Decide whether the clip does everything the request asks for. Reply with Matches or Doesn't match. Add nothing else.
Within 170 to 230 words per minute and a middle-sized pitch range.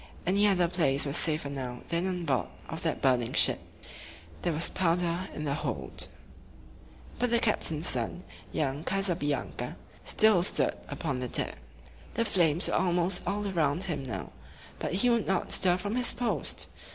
Matches